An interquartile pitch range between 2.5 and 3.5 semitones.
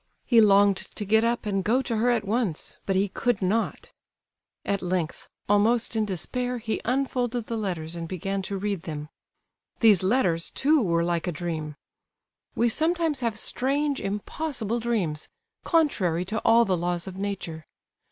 No: average, 4.8 semitones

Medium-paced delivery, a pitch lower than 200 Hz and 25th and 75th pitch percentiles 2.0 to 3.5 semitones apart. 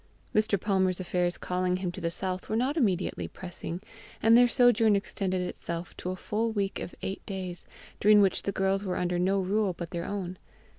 Yes: average, 195 wpm; high, 190 Hz; narrow, 2.5 semitones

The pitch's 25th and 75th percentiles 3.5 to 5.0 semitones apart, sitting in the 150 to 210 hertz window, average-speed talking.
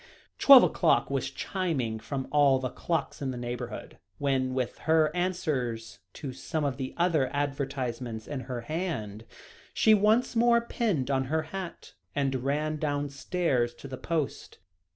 No: average, 4.5 semitones; medium, 140 Hz; average, 150 wpm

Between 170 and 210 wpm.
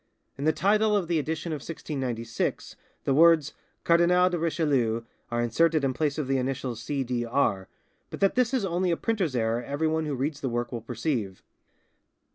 Yes: average, 185 wpm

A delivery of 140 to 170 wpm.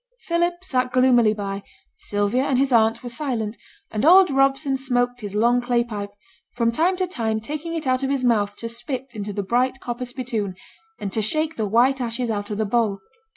No: average, 200 wpm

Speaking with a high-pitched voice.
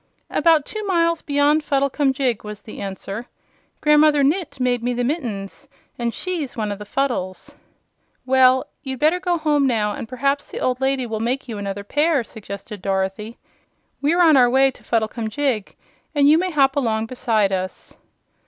Yes: very high, 260 Hz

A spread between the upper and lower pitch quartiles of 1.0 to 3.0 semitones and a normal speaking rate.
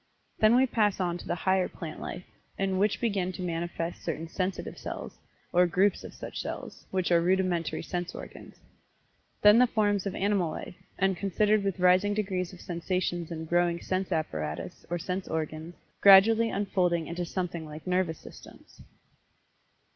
Yes: narrow, 2.4 semitones; average, 160 wpm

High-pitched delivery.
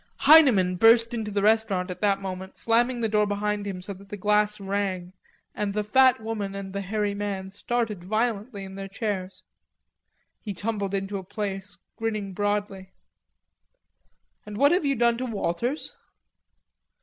Yes: high, 205 Hz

